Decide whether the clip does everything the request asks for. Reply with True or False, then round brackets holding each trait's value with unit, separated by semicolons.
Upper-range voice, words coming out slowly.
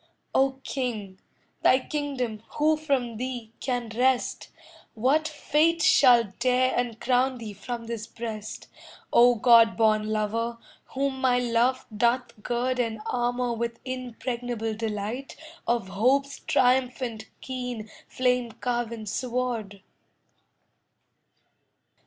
True (245 Hz; 105 wpm)